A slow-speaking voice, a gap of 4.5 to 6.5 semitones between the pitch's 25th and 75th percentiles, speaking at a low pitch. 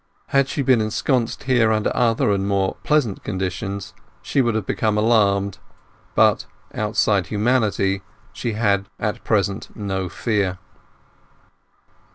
No: slow, 125 wpm; average, 2.8 semitones; low, 105 Hz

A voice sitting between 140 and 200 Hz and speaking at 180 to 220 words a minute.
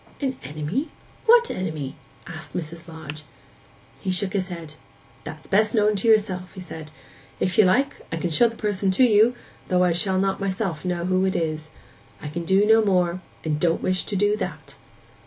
Yes: medium, 185 Hz; average, 190 wpm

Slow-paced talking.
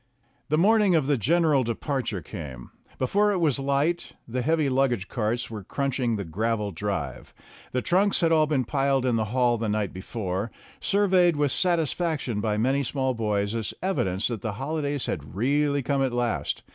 No: average, 180 wpm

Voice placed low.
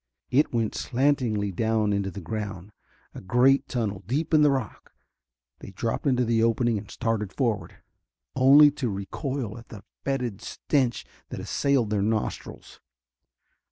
Yes: low, 115 Hz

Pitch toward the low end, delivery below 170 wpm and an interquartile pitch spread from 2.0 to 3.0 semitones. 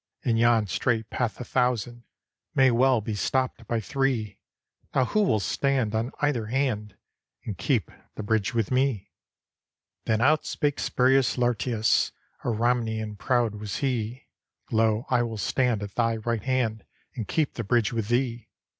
Yes: low, 120 Hz; average, 155 wpm; average, 2.7 semitones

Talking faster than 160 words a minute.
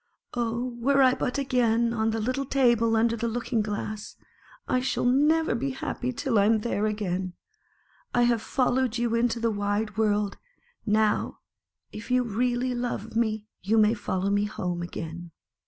Yes: average, 170 wpm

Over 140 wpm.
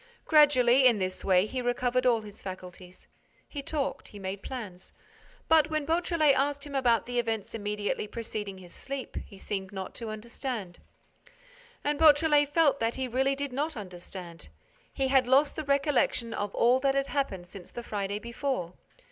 Yes: average, 170 wpm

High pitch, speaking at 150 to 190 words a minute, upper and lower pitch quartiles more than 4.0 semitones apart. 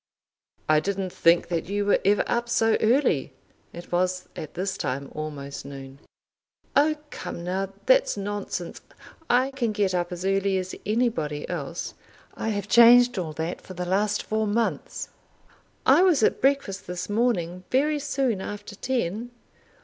Yes: high, 195 Hz; average, 155 wpm; average, 5.2 semitones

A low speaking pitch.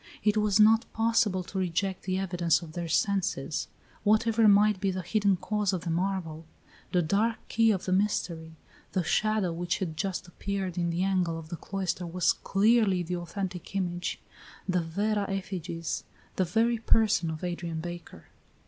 No: medium, 185 Hz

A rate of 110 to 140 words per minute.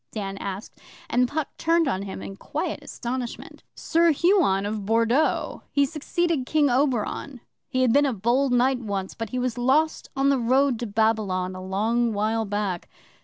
No: average, 170 wpm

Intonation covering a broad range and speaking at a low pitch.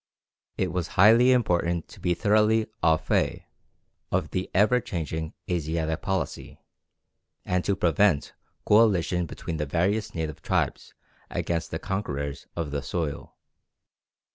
No: average, 4.3 semitones; very low, 90 Hz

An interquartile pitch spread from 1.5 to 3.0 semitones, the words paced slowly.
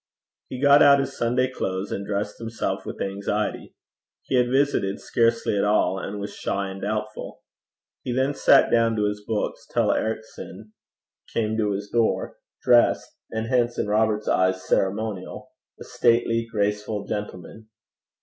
No: narrow, 2.4 semitones; average, 150 wpm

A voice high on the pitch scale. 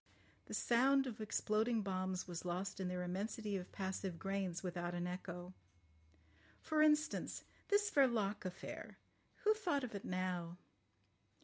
Yes: high, 195 Hz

